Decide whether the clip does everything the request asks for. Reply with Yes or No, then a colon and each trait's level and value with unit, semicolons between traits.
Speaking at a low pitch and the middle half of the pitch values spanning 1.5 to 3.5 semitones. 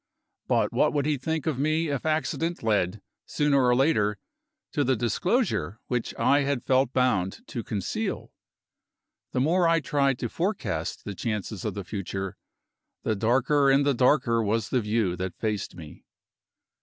No: low, 125 Hz; wide, 5.5 semitones